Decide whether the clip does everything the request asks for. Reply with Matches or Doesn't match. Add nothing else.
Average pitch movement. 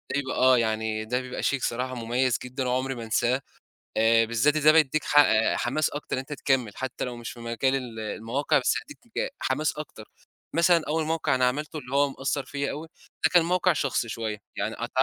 Matches